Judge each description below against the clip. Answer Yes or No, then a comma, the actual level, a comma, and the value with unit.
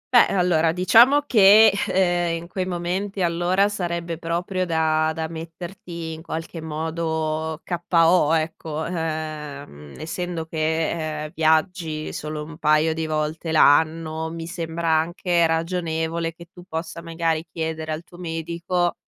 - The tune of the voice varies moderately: No, narrow, 1.7 semitones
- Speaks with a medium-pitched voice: Yes, medium, 165 Hz